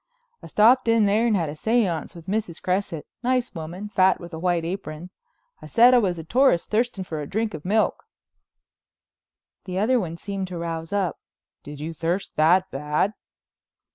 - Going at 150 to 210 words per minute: Yes, average, 180 wpm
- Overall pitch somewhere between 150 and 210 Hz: Yes, medium, 185 Hz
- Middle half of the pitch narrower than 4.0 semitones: No, average, 4.7 semitones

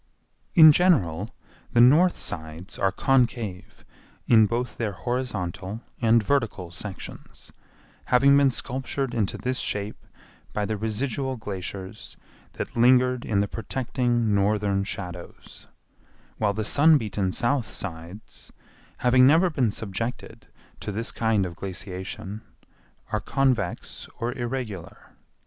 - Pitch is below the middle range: Yes, low, 110 Hz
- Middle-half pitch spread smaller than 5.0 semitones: Yes, average, 4.4 semitones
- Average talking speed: No, slow, 120 wpm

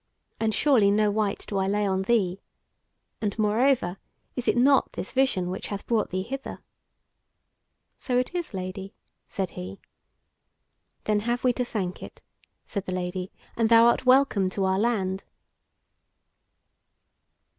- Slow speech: No, average, 145 wpm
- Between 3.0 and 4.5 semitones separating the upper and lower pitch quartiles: Yes, average, 4.1 semitones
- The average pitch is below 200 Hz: No, high, 210 Hz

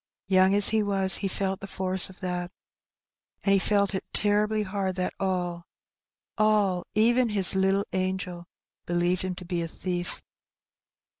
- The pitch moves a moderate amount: No, narrow, 1.8 semitones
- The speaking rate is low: No, average, 165 wpm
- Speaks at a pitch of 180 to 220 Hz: Yes, high, 190 Hz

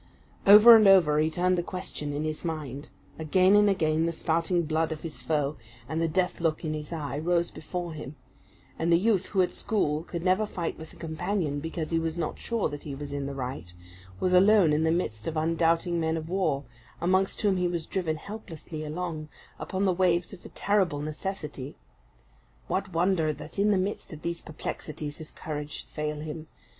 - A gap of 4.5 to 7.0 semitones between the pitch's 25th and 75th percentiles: No, average, 3.0 semitones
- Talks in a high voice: No, medium, 165 Hz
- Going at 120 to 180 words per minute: No, average, 200 wpm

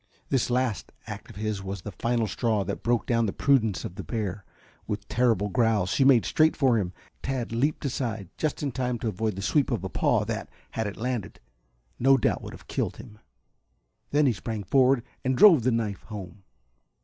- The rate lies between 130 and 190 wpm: No, average, 200 wpm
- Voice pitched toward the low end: Yes, low, 115 Hz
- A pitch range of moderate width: Yes, average, 3.9 semitones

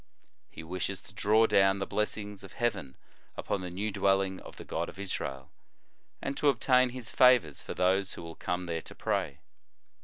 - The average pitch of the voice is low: Yes, very low, 95 Hz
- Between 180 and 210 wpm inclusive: Yes, average, 185 wpm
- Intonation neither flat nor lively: Yes, average, 3.2 semitones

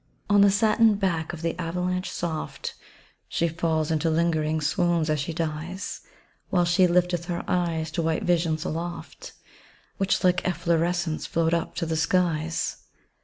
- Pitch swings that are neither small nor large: No, narrow, 1.9 semitones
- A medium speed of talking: Yes, average, 150 wpm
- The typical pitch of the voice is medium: Yes, medium, 170 Hz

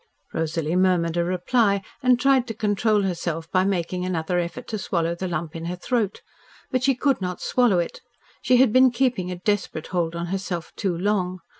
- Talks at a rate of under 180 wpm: No, average, 190 wpm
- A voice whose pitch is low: No, medium, 185 Hz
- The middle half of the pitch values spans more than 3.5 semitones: Yes, average, 4.5 semitones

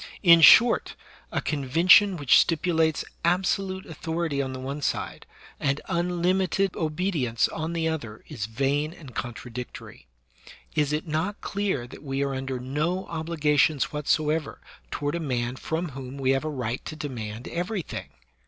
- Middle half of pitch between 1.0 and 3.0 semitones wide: No, average, 4.2 semitones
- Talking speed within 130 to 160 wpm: Yes, average, 150 wpm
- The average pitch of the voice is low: No, medium, 150 Hz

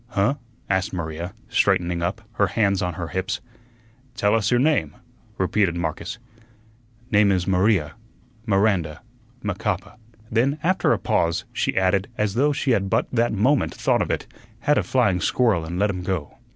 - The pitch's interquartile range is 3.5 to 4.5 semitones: Yes, average, 4.0 semitones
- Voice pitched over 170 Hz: No, low, 100 Hz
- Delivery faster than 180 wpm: No, average, 165 wpm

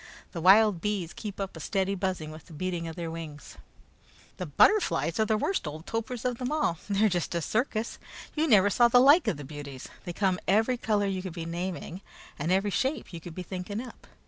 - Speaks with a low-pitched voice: No, high, 190 Hz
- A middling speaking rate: No, fast, 220 wpm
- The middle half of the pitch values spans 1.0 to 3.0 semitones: No, average, 4.7 semitones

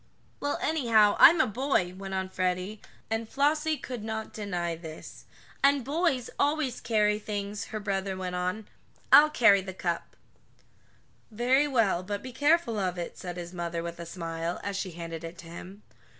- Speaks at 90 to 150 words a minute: No, average, 170 wpm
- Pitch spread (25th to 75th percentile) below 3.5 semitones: No, wide, 5.5 semitones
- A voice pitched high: Yes, high, 205 Hz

